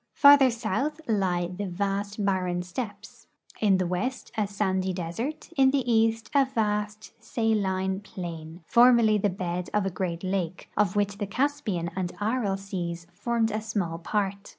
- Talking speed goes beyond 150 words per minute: Yes, average, 160 wpm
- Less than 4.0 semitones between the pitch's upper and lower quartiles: Yes, average, 3.3 semitones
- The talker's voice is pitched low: No, high, 200 Hz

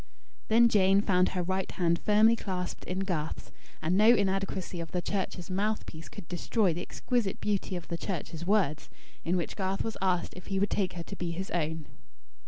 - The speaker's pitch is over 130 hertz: Yes, medium, 185 Hz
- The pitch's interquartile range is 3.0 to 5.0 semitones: No, narrow, 2.5 semitones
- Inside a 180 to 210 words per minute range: Yes, average, 195 wpm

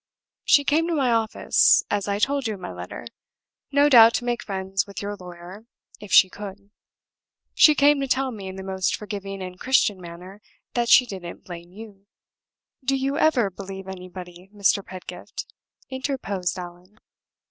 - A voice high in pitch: Yes, high, 200 Hz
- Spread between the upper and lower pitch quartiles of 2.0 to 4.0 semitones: No, average, 4.7 semitones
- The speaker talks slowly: No, average, 170 wpm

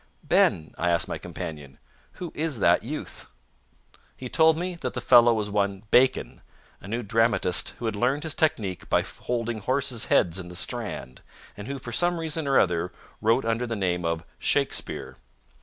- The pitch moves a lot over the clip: Yes, wide, 6.1 semitones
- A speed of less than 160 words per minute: No, average, 175 wpm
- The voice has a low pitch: Yes, low, 115 Hz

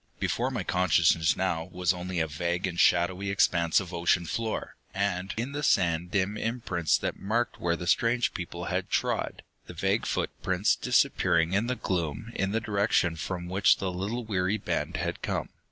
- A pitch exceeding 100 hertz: No, very low, 90 Hz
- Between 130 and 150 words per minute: No, average, 175 wpm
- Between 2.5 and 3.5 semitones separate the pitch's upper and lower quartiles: Yes, average, 3.2 semitones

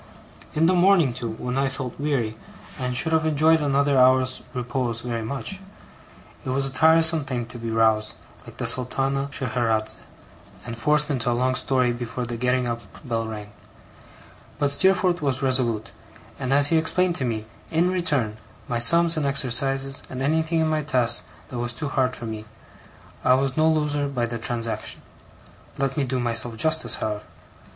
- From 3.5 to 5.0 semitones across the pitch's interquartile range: Yes, average, 3.8 semitones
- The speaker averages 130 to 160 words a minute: No, average, 175 wpm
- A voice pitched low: Yes, low, 130 Hz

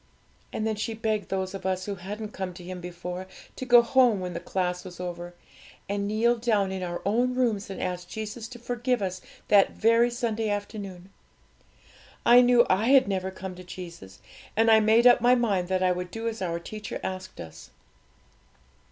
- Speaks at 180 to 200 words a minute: Yes, average, 195 wpm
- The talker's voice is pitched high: Yes, high, 200 Hz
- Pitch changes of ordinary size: Yes, average, 3.8 semitones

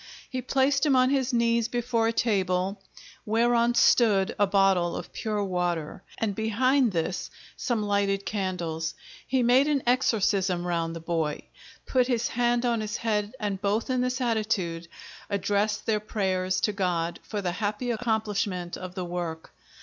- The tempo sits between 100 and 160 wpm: Yes, average, 155 wpm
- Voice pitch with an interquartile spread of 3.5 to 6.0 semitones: Yes, average, 4.4 semitones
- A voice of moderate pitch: No, high, 210 Hz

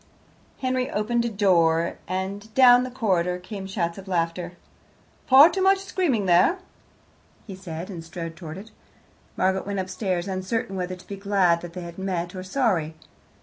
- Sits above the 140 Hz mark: Yes, high, 190 Hz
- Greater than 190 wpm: No, average, 165 wpm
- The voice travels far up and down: No, average, 4.2 semitones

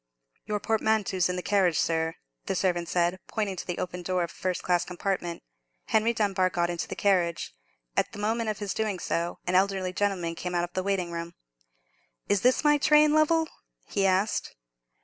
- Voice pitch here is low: No, medium, 185 Hz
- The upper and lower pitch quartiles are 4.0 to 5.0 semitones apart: No, average, 3.1 semitones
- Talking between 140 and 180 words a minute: No, average, 190 wpm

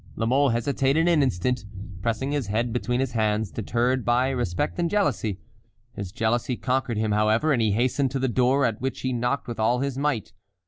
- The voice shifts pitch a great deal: No, average, 3.2 semitones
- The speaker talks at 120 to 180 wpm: No, average, 195 wpm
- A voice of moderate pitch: No, low, 125 Hz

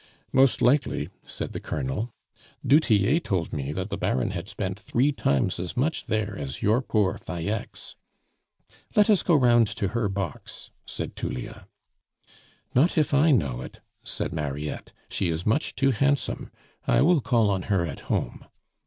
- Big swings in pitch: Yes, wide, 8.1 semitones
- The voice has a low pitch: Yes, low, 105 Hz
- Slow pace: No, average, 160 wpm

